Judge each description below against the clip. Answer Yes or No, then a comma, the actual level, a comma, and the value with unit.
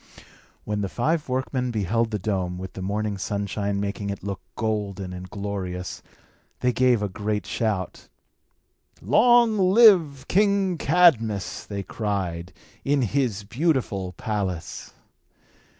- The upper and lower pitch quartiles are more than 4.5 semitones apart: Yes, average, 5.2 semitones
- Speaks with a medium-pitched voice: No, low, 105 Hz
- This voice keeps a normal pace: No, slow, 120 wpm